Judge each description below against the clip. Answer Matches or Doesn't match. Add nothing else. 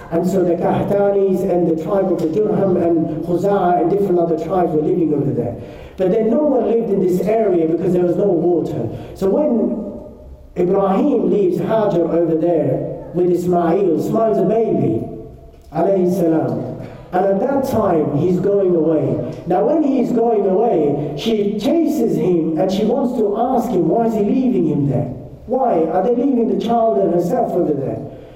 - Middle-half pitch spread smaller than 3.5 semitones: Doesn't match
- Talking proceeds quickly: Doesn't match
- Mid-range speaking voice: Matches